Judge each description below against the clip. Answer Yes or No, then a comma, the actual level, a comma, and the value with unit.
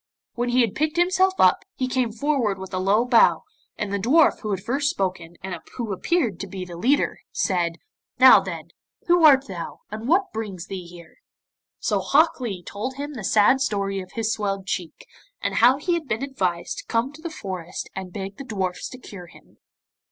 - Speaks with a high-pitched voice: Yes, high, 220 Hz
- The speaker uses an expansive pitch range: Yes, wide, 6.3 semitones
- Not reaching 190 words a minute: No, fast, 205 wpm